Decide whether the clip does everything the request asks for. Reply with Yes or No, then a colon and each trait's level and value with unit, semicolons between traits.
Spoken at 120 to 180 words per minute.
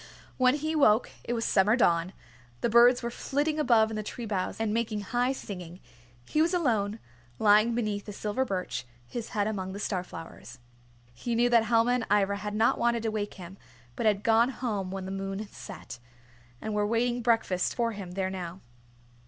No: average, 195 wpm